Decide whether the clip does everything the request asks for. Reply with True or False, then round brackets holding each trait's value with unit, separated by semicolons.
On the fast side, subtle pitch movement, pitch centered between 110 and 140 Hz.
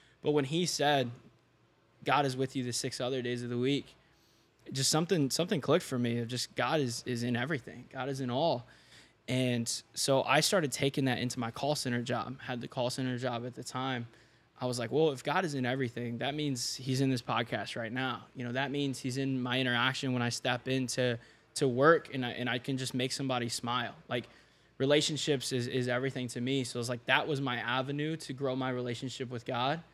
True (225 wpm; 2.2 semitones; 130 Hz)